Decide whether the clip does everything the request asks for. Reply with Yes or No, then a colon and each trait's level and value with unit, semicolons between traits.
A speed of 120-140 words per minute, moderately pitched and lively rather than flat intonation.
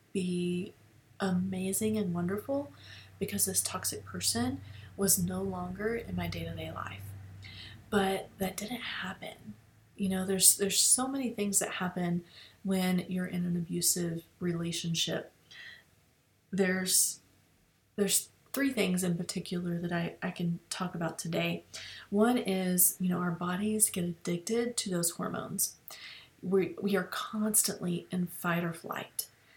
No: slow, 135 wpm; medium, 180 Hz; average, 2.7 semitones